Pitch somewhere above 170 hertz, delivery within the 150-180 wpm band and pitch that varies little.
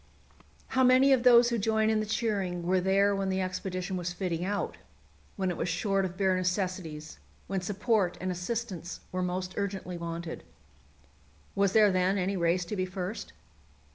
Yes: high, 190 Hz; average, 170 wpm; narrow, 2.3 semitones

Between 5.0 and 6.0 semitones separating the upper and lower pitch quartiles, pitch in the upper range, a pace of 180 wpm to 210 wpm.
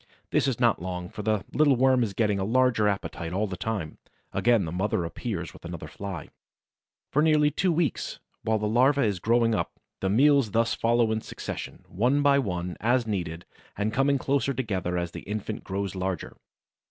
No: average, 5.3 semitones; low, 110 Hz; average, 190 wpm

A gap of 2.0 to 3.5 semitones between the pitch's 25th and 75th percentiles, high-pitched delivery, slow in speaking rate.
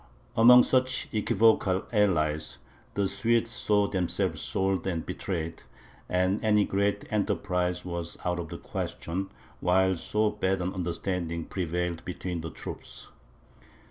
No: average, 2.8 semitones; very low, 95 Hz; slow, 125 wpm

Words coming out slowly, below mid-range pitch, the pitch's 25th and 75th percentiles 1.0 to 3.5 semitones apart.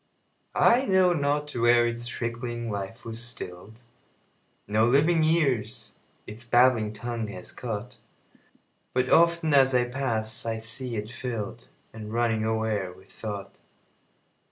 Yes: slow, 115 wpm; low, 120 Hz; average, 2.7 semitones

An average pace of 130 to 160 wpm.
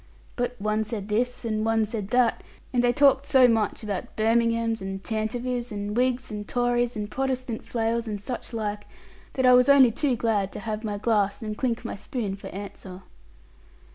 No: average, 185 wpm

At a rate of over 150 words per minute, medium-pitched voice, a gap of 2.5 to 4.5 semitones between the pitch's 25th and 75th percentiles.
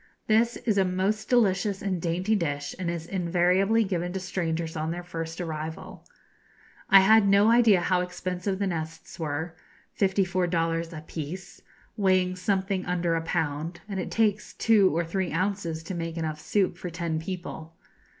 Yes: average, 165 wpm; medium, 180 Hz; average, 2.9 semitones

